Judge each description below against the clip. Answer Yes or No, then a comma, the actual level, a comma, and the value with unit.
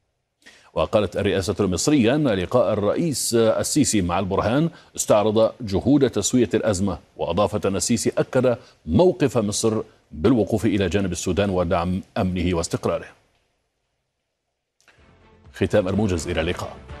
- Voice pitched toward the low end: Yes, low, 100 Hz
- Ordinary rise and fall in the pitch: Yes, average, 3.9 semitones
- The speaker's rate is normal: Yes, average, 105 wpm